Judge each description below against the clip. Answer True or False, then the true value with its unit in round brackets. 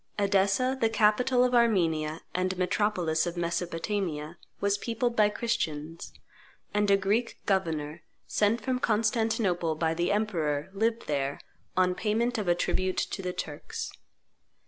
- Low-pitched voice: False (195 Hz)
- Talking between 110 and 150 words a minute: True (135 wpm)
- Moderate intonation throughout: True (4.8 semitones)